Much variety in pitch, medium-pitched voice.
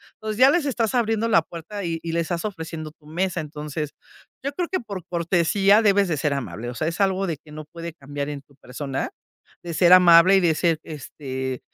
No: average, 4.5 semitones; medium, 170 Hz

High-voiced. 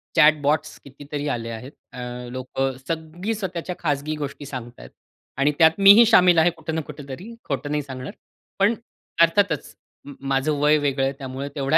No: medium, 150 Hz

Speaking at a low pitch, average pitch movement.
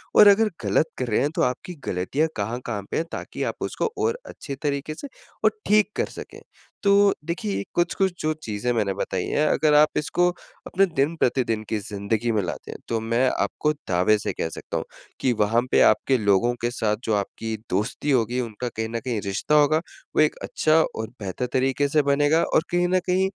No: low, 130 Hz; wide, 6.1 semitones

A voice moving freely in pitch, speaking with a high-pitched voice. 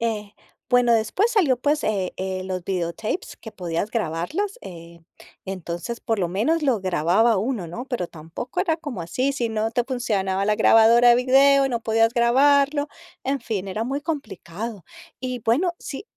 Yes: wide, 5.9 semitones; high, 230 Hz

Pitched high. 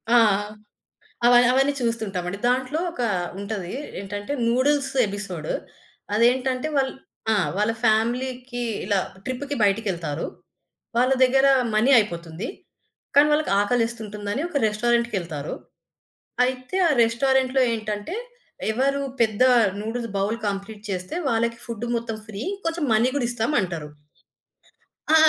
Yes: high, 230 Hz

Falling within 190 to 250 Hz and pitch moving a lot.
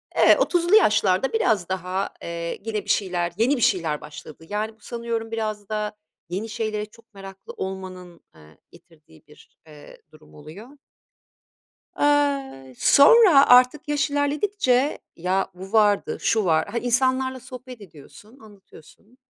Yes: high, 215 Hz; wide, 5.8 semitones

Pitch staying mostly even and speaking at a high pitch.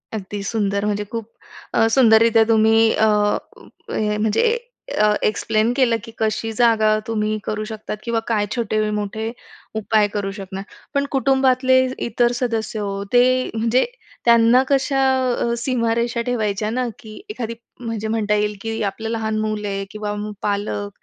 Yes: narrow, 1.8 semitones; high, 220 Hz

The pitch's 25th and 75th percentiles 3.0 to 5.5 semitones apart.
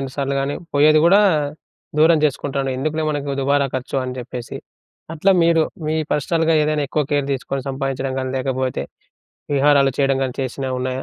No: narrow, 2.5 semitones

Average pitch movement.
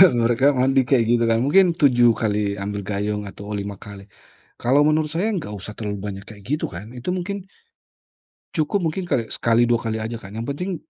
No: wide, 5.7 semitones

